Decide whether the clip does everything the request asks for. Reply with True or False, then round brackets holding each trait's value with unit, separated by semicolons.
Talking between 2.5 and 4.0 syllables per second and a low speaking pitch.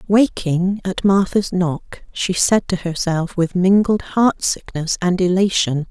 False (3.7 syllables/s; 185 Hz)